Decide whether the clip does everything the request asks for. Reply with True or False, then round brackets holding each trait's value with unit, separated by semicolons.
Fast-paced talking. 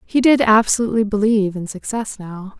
False (160 wpm)